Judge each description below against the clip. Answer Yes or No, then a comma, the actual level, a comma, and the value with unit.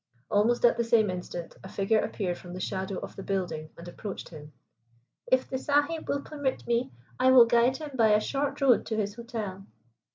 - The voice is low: No, high, 225 Hz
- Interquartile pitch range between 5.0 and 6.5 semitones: Yes, average, 5.3 semitones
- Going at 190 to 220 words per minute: Yes, average, 200 wpm